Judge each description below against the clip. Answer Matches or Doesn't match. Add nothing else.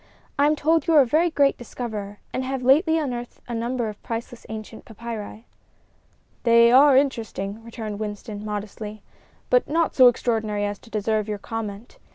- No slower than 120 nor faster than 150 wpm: Doesn't match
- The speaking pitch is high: Matches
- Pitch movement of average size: Matches